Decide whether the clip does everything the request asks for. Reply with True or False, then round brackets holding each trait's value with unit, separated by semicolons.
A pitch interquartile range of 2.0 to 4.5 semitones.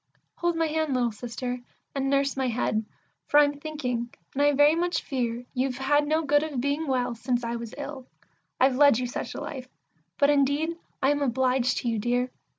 True (2.8 semitones)